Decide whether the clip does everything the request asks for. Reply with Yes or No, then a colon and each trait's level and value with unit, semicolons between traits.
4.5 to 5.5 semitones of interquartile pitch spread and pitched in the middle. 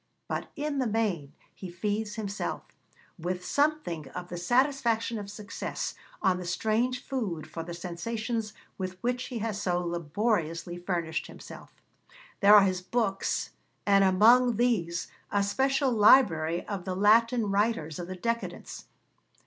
No: average, 4.8 semitones; high, 200 Hz